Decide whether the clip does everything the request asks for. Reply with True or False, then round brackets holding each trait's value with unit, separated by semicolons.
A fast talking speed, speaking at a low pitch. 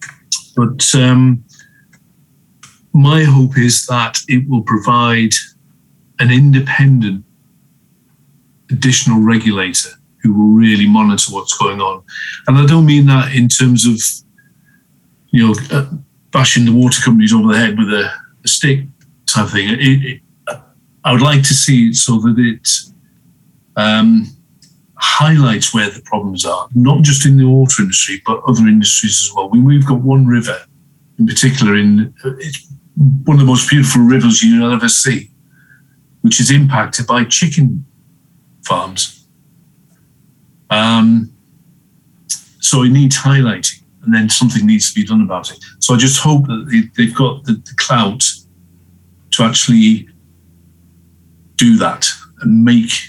False (145 wpm; 130 Hz)